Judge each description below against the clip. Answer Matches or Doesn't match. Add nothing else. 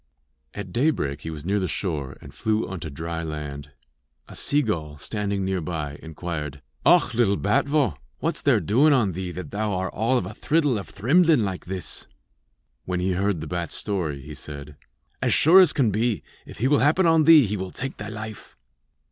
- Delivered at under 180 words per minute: Doesn't match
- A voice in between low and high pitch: Doesn't match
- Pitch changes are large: Matches